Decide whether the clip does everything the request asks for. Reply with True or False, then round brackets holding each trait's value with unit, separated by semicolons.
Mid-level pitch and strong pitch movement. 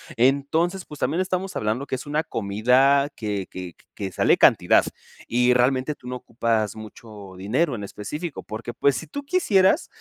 False (125 Hz; 5.9 semitones)